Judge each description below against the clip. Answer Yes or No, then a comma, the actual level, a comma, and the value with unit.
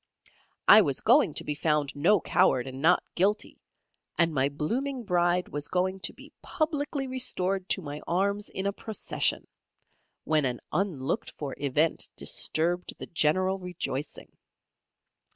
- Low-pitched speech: No, medium, 180 Hz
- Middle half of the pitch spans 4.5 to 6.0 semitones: Yes, average, 4.9 semitones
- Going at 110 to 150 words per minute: Yes, average, 140 wpm